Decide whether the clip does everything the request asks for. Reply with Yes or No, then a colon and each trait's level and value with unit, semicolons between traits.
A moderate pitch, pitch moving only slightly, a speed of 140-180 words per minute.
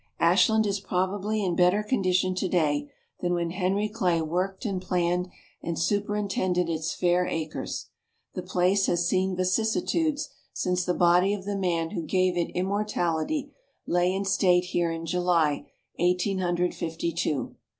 Yes: medium, 180 Hz; narrow, 2.2 semitones; average, 150 wpm